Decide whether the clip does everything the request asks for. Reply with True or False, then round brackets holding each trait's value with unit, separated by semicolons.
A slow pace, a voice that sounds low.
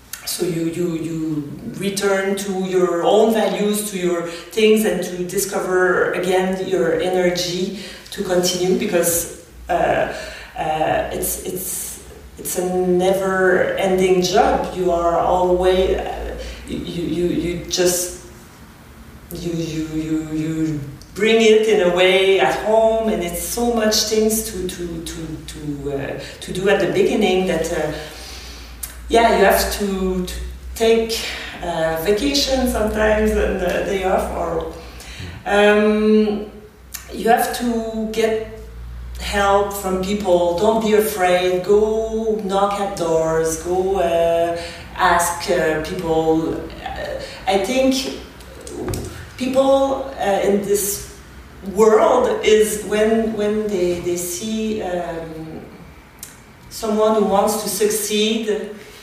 False (120 wpm; 185 Hz)